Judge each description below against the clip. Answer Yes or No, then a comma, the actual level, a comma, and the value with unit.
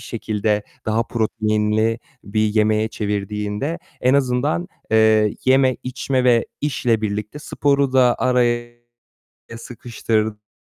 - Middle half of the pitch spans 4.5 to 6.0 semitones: No, average, 3.0 semitones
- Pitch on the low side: Yes, low, 115 Hz